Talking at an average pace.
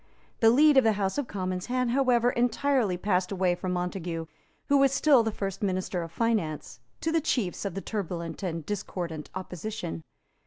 Yes: average, 180 wpm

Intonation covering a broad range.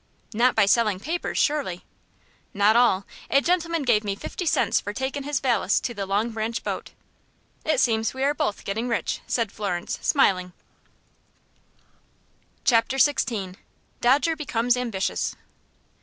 No: average, 5.0 semitones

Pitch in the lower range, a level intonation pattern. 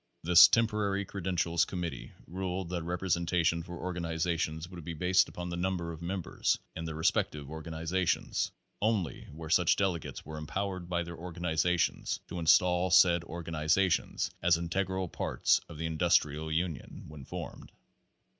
Yes: very low, 85 Hz; narrow, 2.0 semitones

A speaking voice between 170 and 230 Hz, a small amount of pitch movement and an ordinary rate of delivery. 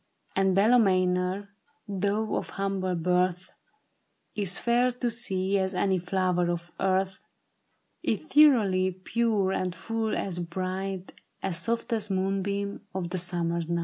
No: high, 190 Hz; narrow, 1.8 semitones; slow, 125 wpm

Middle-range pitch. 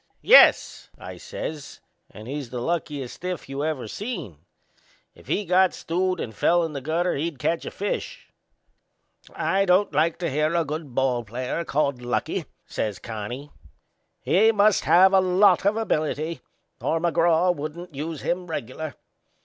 Yes: medium, 160 Hz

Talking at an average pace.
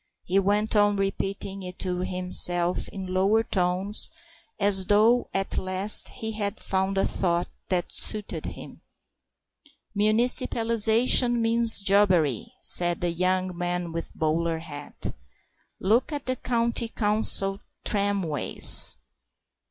No: slow, 120 wpm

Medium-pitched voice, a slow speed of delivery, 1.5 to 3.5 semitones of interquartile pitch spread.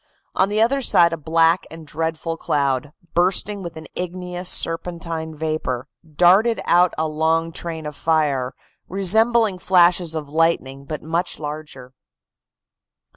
Yes: medium, 165 Hz; slow, 130 wpm; narrow, 2.6 semitones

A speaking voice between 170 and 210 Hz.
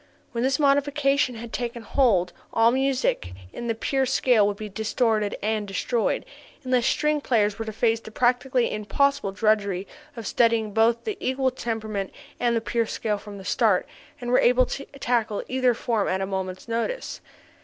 No: high, 230 Hz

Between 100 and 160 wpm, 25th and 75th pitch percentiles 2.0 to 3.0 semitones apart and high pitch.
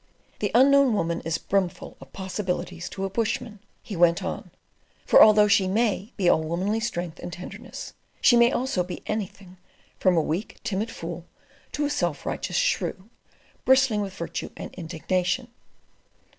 No: average, 155 wpm; average, 4.2 semitones; high, 195 Hz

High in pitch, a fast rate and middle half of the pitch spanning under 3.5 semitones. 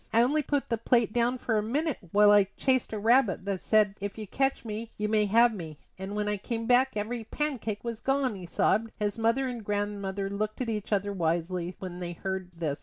Yes: high, 210 Hz; fast, 225 wpm; average, 3.1 semitones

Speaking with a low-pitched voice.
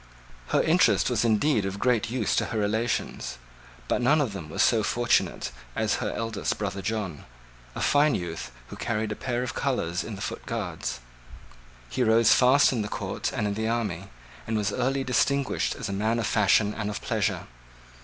Yes: low, 110 Hz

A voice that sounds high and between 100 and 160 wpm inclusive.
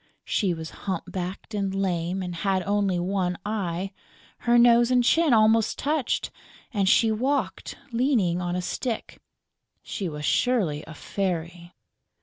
Yes: high, 195 Hz; average, 140 wpm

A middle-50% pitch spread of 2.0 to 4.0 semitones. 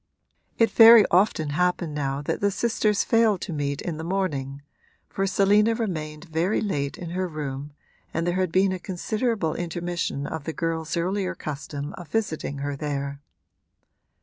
No: average, 4.8 semitones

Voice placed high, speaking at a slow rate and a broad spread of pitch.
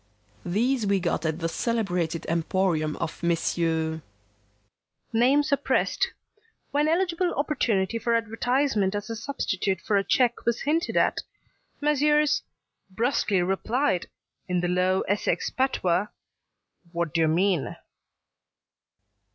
Yes: high, 200 Hz; slow, 105 wpm; wide, 7.0 semitones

